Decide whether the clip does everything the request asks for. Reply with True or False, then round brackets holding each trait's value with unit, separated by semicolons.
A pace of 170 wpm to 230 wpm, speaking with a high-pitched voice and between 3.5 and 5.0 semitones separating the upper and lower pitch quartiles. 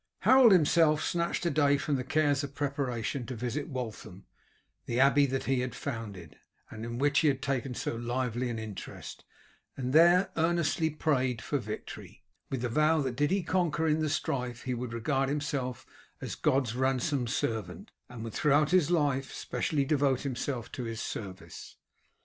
False (175 wpm; 135 Hz; 3.8 semitones)